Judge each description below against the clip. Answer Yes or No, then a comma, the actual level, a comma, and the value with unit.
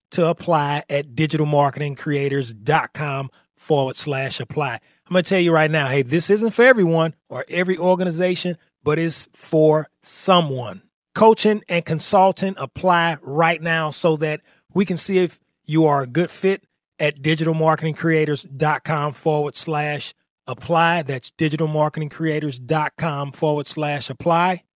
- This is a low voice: No, medium, 155 Hz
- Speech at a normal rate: No, slow, 125 wpm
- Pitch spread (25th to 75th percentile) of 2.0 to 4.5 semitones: Yes, average, 2.8 semitones